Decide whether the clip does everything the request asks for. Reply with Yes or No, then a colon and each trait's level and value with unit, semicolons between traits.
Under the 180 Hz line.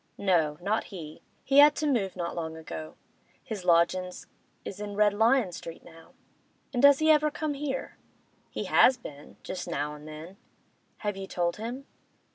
No: high, 195 Hz